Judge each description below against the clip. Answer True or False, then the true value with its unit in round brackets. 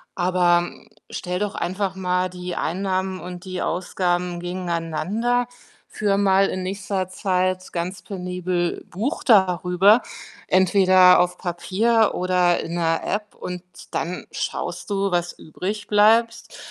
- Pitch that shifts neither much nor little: False (1.9 semitones)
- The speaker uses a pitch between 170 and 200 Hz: True (185 Hz)